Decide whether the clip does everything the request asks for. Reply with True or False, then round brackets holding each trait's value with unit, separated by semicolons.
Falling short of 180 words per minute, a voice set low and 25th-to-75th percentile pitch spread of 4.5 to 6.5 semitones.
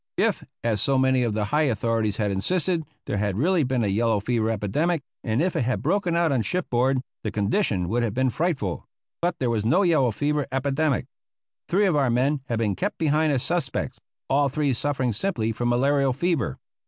False (200 wpm; 130 Hz; 5.4 semitones)